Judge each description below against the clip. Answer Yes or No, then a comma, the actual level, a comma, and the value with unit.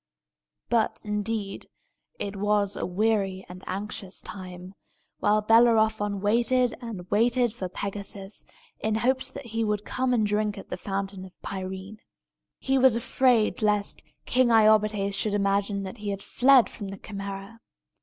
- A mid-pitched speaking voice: No, high, 210 Hz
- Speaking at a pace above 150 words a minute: No, average, 145 wpm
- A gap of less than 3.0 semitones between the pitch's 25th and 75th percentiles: Yes, narrow, 2.4 semitones